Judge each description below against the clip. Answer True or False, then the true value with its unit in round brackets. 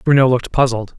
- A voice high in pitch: False (125 Hz)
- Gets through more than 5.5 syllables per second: True (6.7 syllables/s)